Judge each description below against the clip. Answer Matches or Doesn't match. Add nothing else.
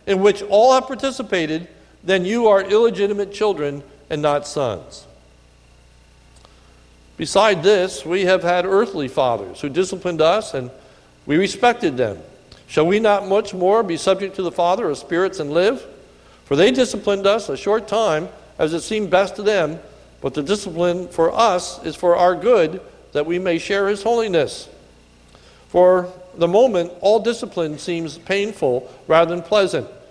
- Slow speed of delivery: Doesn't match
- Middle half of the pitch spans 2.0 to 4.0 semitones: Doesn't match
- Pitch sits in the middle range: Matches